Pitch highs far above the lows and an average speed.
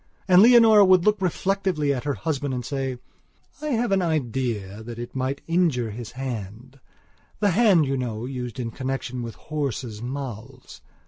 Yes: wide, 6.4 semitones; average, 155 wpm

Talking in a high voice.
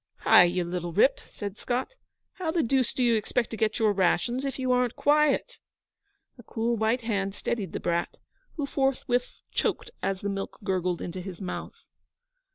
Yes: high, 225 Hz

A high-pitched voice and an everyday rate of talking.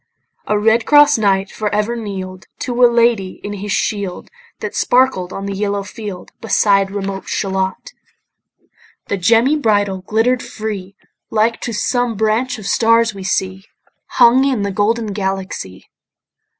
Yes: high, 210 Hz; average, 145 wpm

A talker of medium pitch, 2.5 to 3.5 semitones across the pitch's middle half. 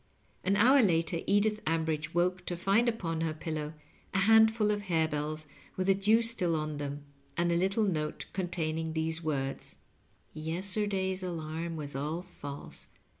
No: medium, 170 Hz; average, 3.9 semitones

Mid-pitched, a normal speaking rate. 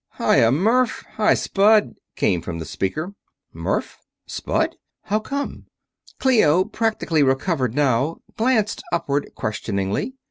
No: medium, 165 Hz; slow, 115 wpm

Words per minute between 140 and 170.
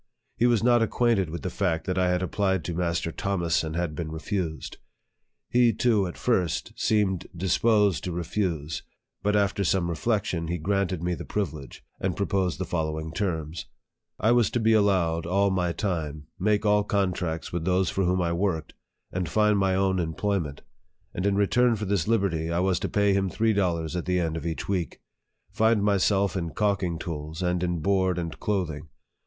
No: average, 190 wpm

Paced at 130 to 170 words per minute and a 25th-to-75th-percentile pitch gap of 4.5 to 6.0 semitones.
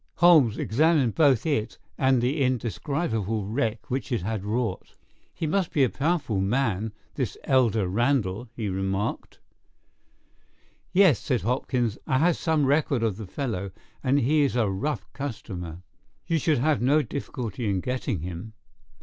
Yes: average, 150 wpm; average, 5.1 semitones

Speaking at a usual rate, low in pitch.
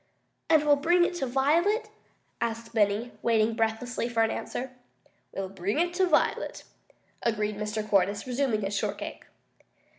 No: average, 145 wpm; high, 230 Hz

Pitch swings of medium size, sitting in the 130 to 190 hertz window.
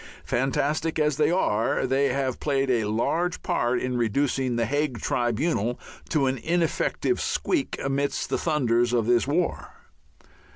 Yes: average, 4.0 semitones; low, 135 Hz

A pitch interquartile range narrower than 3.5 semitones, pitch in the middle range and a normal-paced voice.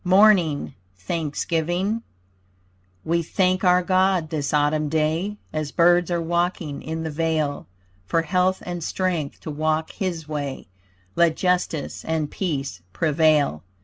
No: average, 2.8 semitones; medium, 165 Hz; slow, 125 wpm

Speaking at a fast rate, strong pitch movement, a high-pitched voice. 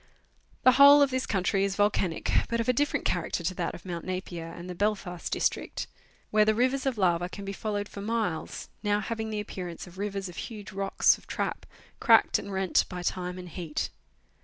No: fast, 210 wpm; average, 3.4 semitones; high, 195 Hz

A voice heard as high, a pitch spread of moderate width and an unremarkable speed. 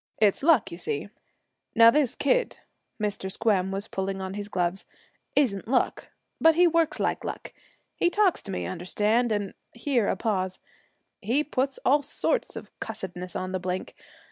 No: high, 210 Hz; wide, 6.3 semitones; average, 165 wpm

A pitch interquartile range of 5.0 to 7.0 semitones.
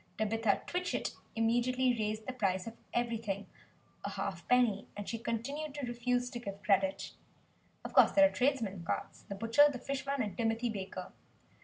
No: average, 3.7 semitones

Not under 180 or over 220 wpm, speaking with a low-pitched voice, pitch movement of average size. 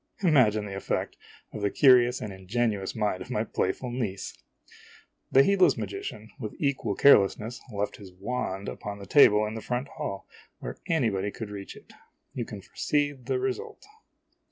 No: average, 160 wpm; low, 110 Hz; average, 4.2 semitones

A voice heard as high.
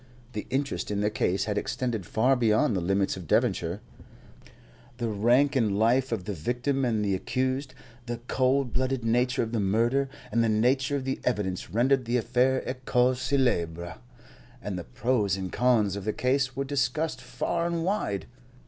No: low, 120 Hz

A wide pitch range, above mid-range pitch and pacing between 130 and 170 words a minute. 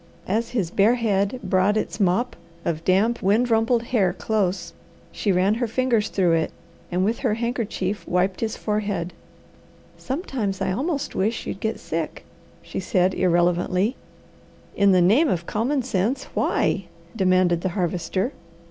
No: average, 4.0 semitones; high, 200 Hz; average, 150 wpm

